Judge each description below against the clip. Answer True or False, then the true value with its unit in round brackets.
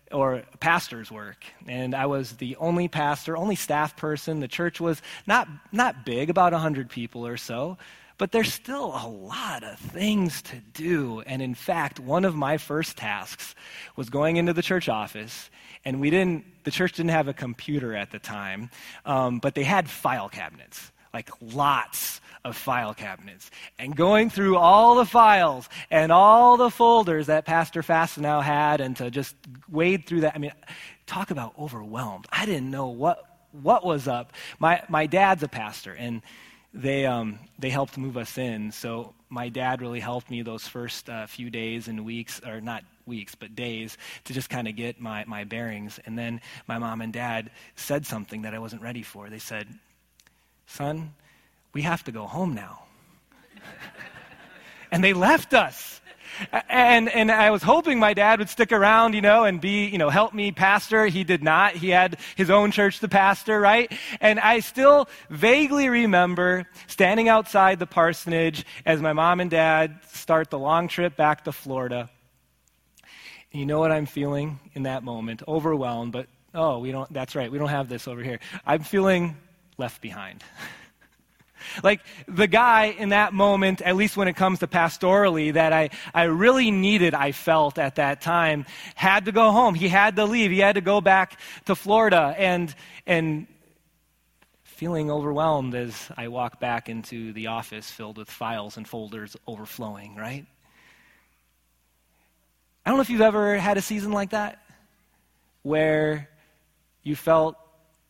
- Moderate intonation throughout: False (7.6 semitones)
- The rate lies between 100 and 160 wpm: False (175 wpm)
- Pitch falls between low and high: True (155 Hz)